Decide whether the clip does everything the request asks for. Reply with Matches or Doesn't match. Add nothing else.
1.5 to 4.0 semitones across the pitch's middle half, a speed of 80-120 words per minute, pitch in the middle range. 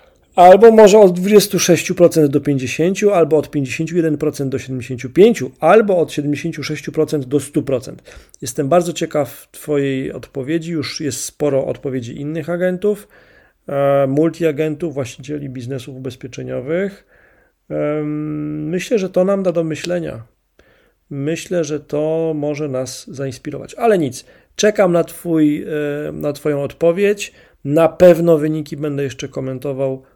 Matches